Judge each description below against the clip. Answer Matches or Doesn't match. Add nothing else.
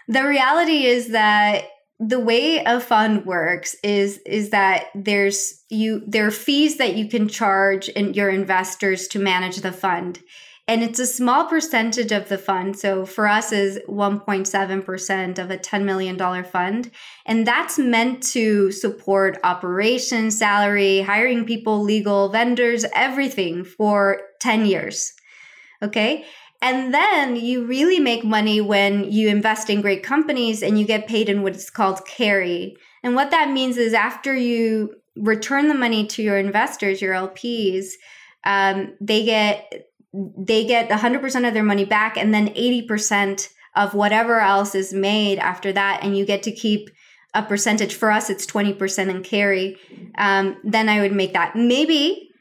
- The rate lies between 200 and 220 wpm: Doesn't match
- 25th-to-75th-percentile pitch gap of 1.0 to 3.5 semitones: Matches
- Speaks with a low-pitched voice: Doesn't match